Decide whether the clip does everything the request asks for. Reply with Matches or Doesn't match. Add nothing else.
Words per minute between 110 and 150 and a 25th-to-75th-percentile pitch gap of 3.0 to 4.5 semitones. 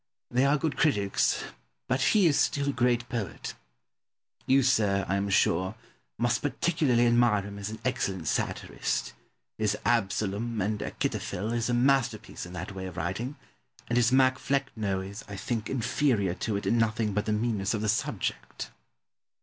Doesn't match